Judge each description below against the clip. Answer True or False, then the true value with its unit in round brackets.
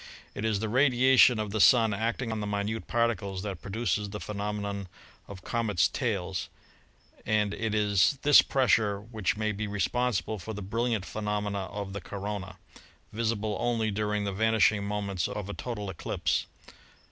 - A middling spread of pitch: False (1.9 semitones)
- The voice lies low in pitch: True (105 Hz)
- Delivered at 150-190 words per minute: True (160 wpm)